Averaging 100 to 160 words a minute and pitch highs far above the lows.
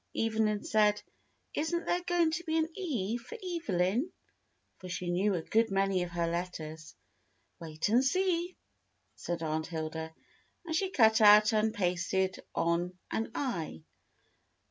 Yes: average, 145 wpm; wide, 8.2 semitones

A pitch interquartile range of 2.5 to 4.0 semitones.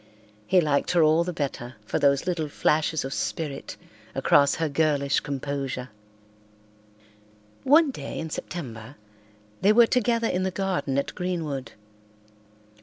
No: average, 4.5 semitones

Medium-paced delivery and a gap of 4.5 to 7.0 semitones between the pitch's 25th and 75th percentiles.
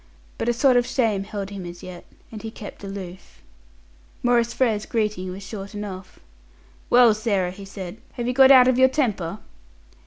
No: average, 180 wpm; average, 3.8 semitones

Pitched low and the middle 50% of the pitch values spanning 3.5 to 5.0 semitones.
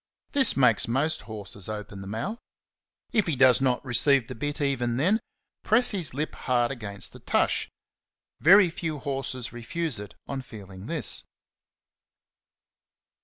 No: low, 130 Hz; wide, 5.6 semitones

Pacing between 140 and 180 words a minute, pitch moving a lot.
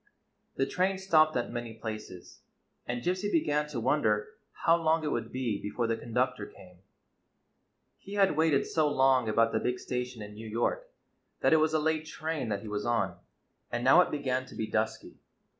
No: average, 190 wpm; wide, 5.8 semitones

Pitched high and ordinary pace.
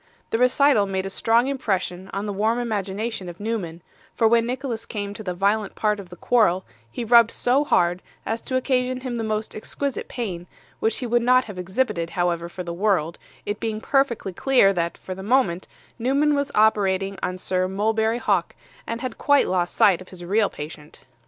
Yes: high, 210 Hz; average, 195 wpm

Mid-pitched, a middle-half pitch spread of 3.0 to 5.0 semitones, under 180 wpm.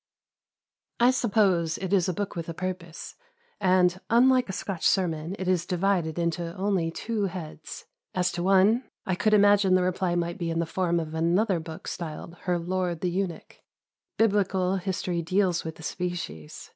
No: medium, 180 Hz; narrow, 2.4 semitones; average, 170 wpm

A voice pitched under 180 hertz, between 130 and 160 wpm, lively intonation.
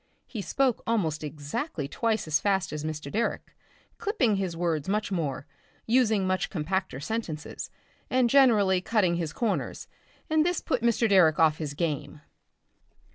No: high, 190 Hz; average, 145 wpm; wide, 6.7 semitones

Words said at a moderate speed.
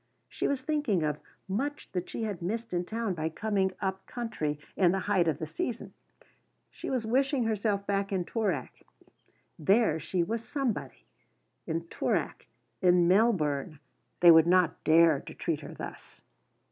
Yes: average, 160 wpm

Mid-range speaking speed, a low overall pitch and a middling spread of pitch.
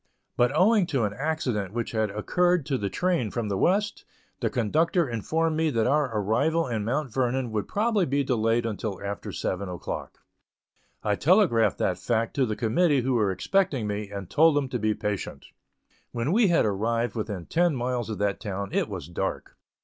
No: average, 190 wpm; low, 120 Hz; wide, 6.8 semitones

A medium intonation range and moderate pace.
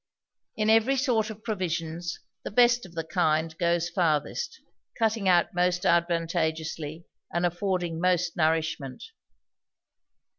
No: average, 4.0 semitones; slow, 115 wpm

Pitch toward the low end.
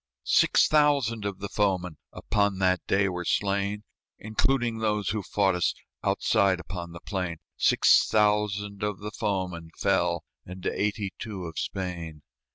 Yes: low, 100 Hz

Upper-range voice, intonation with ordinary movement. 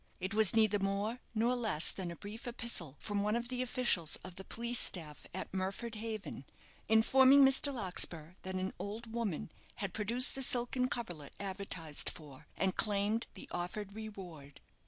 Yes: high, 205 Hz; average, 4.1 semitones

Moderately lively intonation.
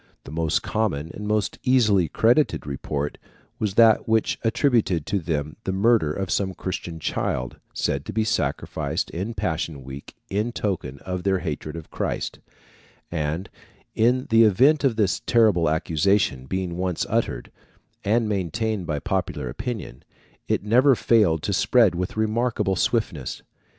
No: wide, 5.7 semitones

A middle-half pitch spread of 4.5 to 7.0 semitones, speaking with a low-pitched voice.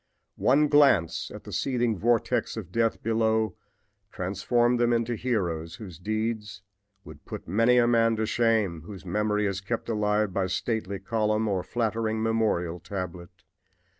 No: average, 3.2 semitones; low, 110 Hz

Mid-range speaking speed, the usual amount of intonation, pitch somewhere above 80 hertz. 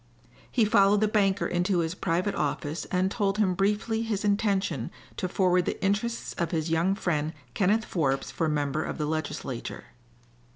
Yes: average, 165 wpm; average, 4.3 semitones; medium, 185 Hz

